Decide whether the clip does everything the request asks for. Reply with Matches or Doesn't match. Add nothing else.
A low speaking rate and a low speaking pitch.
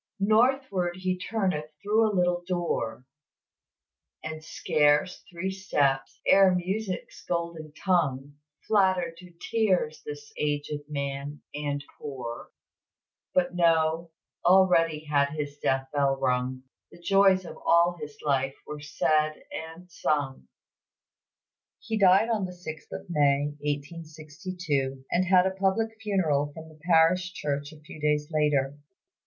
Doesn't match